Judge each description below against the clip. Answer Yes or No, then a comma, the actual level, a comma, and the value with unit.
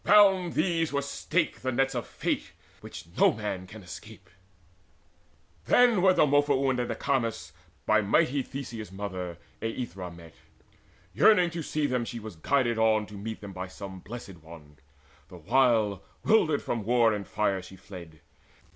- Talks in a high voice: No, low, 115 Hz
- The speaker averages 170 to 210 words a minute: No, average, 155 wpm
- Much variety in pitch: Yes, wide, 6.5 semitones